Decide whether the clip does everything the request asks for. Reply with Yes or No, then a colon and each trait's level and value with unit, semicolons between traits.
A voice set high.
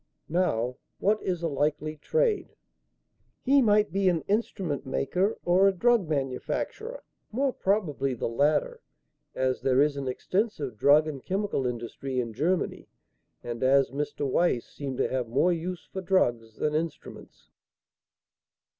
No: medium, 155 Hz